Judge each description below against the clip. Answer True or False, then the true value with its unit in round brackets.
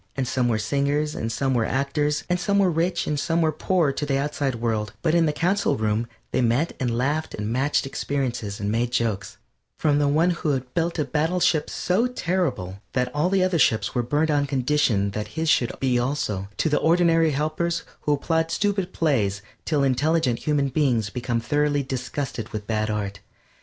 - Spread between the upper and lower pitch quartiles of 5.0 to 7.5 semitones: True (5.3 semitones)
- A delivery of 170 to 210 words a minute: True (200 wpm)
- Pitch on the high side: False (140 Hz)